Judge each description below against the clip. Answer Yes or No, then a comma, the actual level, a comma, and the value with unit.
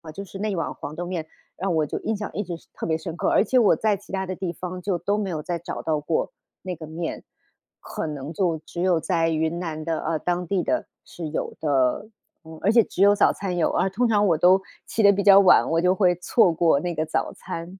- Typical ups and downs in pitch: Yes, average, 3.2 semitones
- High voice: No, medium, 175 Hz